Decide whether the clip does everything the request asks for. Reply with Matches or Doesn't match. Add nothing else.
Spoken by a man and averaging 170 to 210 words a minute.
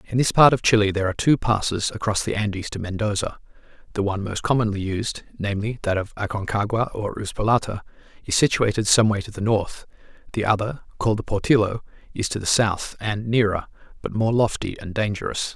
Matches